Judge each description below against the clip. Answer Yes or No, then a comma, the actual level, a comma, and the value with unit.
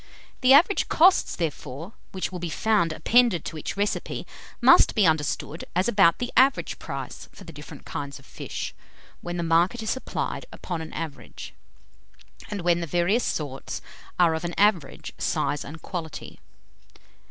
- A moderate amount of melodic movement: Yes, average, 4.6 semitones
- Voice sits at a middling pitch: Yes, medium, 175 Hz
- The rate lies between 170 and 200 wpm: No, average, 160 wpm